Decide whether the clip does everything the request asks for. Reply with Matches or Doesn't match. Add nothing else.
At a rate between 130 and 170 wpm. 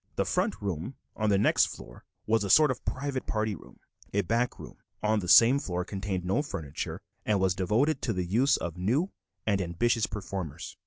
Doesn't match